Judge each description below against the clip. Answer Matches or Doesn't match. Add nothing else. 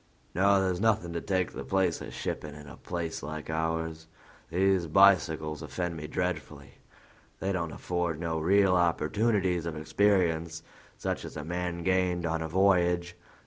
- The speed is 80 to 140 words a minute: Doesn't match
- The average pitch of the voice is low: Matches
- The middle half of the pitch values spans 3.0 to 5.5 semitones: Doesn't match